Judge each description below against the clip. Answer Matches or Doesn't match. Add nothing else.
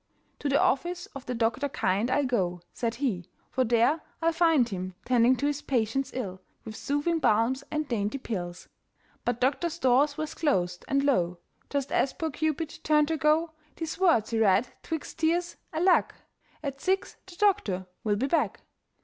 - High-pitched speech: Matches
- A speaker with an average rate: Matches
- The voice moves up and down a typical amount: Doesn't match